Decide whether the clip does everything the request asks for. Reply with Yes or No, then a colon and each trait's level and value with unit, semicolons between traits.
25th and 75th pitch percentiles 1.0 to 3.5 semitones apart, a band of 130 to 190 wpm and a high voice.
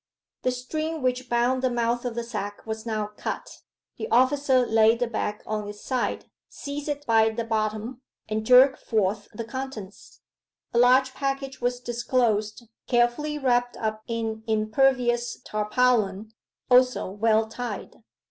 Yes: average, 2.8 semitones; average, 145 wpm; high, 240 Hz